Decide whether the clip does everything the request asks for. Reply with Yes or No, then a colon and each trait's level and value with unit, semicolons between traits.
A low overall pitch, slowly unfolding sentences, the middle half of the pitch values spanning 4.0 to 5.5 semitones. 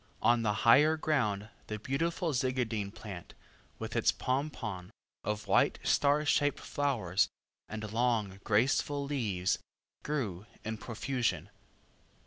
Yes: low, 115 Hz; slow, 115 wpm; average, 5.2 semitones